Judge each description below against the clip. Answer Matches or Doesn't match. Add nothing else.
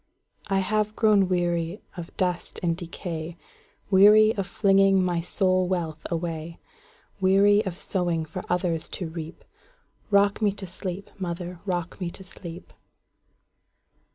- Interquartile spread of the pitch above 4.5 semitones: Doesn't match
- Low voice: Doesn't match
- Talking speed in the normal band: Doesn't match